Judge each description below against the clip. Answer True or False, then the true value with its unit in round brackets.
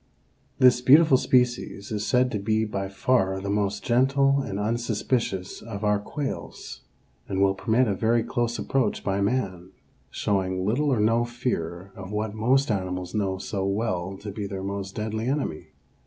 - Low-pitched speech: True (105 Hz)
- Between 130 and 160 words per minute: False (170 wpm)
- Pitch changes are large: False (4.0 semitones)